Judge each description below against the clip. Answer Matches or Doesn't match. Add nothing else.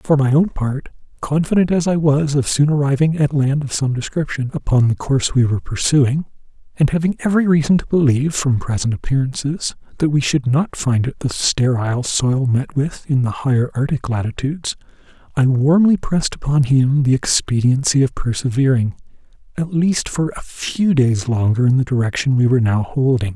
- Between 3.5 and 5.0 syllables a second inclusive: Doesn't match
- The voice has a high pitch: Doesn't match